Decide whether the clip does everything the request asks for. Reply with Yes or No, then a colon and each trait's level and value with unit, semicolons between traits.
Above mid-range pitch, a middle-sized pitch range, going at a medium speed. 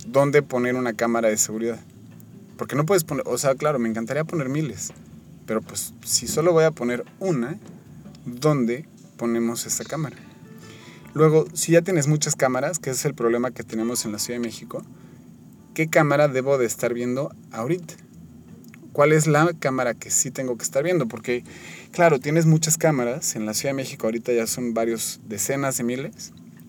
No: low, 130 Hz; average, 4.9 semitones; average, 180 wpm